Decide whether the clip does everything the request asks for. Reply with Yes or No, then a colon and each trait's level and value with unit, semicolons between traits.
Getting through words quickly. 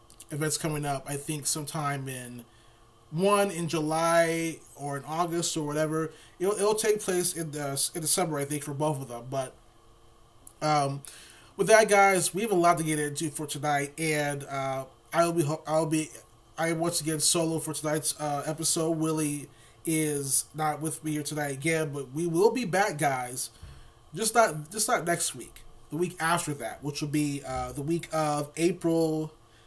No: average, 180 wpm